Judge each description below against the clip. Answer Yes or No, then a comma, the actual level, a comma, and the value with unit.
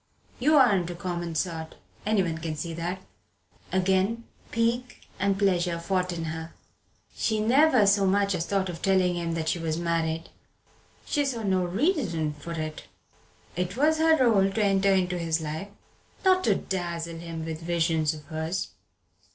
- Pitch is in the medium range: Yes, medium, 180 Hz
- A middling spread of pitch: Yes, average, 3.4 semitones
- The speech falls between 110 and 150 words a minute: No, average, 160 wpm